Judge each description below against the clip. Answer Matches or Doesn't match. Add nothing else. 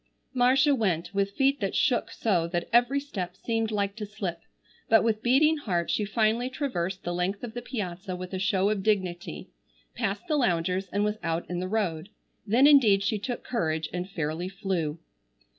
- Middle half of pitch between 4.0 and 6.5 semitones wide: Matches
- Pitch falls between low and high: Doesn't match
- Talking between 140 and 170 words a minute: Doesn't match